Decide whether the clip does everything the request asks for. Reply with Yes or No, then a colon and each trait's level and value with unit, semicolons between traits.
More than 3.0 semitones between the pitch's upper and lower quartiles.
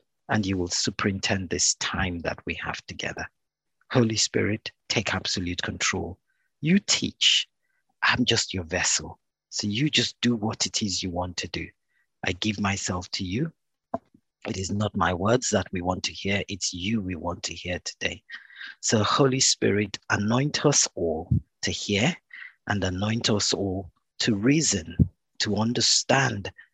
Yes: average, 3.8 semitones